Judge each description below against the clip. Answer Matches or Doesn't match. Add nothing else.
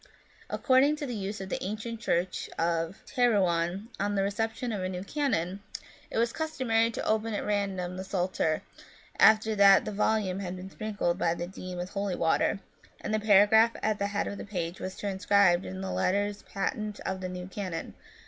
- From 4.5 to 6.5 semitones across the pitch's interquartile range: Doesn't match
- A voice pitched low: Doesn't match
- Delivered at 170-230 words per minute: Matches